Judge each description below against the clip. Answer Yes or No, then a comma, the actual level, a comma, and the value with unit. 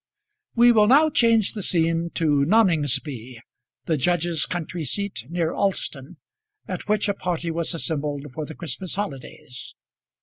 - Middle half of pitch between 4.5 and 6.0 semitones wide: Yes, average, 5.0 semitones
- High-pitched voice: No, medium, 170 Hz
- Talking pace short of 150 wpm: Yes, average, 140 wpm